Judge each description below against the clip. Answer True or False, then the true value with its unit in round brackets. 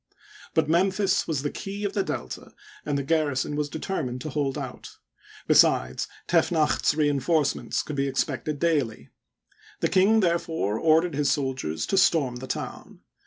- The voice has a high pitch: False (150 Hz)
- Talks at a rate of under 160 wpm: False (165 wpm)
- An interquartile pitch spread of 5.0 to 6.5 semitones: False (4.0 semitones)